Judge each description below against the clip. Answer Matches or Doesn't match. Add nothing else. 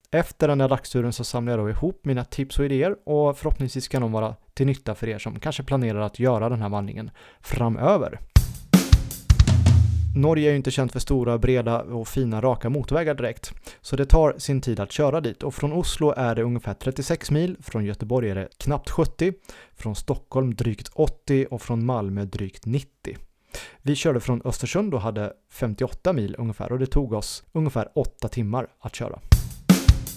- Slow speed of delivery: Doesn't match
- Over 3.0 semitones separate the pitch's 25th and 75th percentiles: Matches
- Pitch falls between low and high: Doesn't match